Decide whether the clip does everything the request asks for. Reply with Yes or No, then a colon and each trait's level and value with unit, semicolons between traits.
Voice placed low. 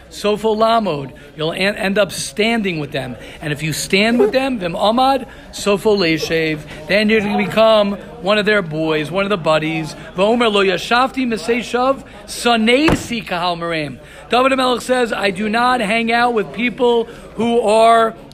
No: high, 210 Hz